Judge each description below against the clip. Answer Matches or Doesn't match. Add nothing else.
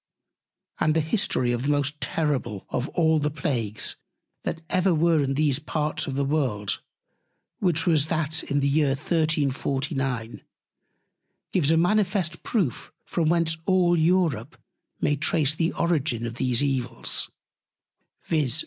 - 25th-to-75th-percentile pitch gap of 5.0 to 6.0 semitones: Doesn't match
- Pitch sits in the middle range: Matches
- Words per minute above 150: Doesn't match